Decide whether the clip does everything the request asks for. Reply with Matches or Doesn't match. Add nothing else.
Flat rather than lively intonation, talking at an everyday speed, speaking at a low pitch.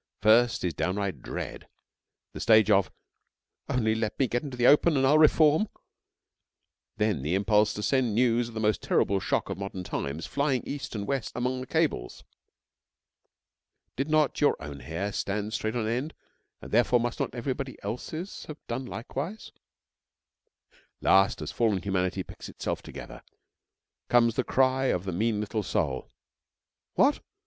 Doesn't match